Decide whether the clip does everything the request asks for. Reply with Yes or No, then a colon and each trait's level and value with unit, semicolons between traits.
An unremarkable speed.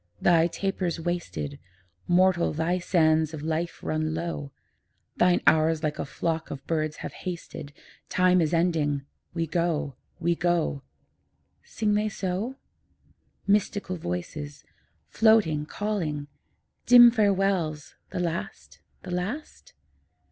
No: slow, 115 wpm